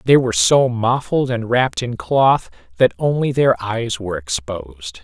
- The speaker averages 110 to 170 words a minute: Yes, average, 165 wpm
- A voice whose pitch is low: Yes, low, 110 Hz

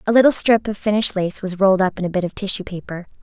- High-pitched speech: Yes, high, 195 Hz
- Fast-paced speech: Yes, fast, 280 wpm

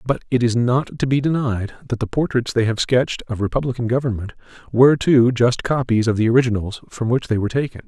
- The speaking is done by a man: Yes, male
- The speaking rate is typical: No, fast, 215 wpm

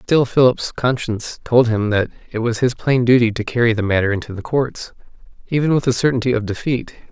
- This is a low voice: Yes, low, 120 Hz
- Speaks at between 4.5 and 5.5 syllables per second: No, 5.7 syllables/s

